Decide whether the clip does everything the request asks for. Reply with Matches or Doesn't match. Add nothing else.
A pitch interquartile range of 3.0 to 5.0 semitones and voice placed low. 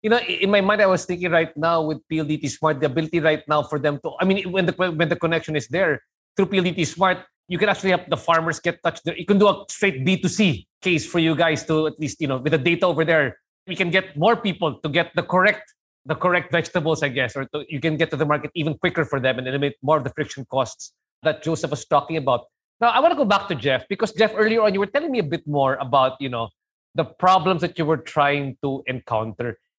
Doesn't match